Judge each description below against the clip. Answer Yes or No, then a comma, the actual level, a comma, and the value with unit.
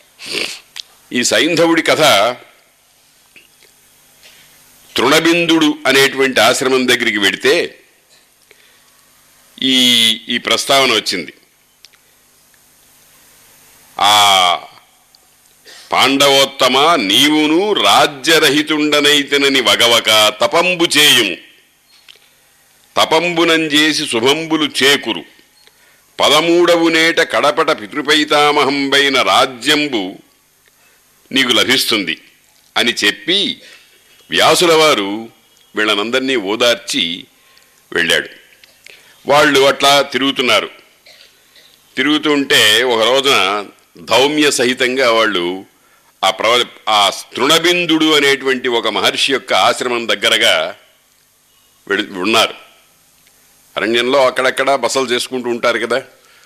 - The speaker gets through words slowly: Yes, slow, 65 wpm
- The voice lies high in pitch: No, medium, 140 Hz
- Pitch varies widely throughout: No, average, 3.6 semitones